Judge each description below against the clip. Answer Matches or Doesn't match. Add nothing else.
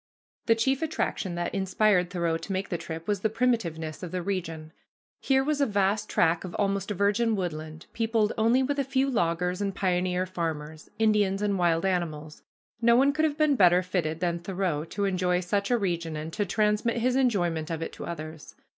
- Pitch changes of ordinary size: Matches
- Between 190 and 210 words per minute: Matches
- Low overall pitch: Doesn't match